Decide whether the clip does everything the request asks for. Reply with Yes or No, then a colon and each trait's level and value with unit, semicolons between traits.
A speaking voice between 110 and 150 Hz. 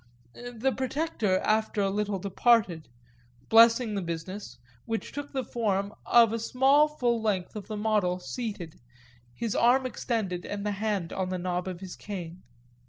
No: high, 210 Hz